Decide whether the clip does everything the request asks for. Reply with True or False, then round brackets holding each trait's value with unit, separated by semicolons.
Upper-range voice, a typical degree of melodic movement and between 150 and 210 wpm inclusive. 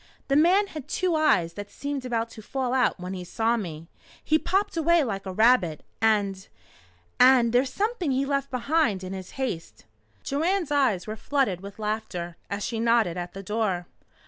False (230 Hz; 6.4 semitones; 180 wpm)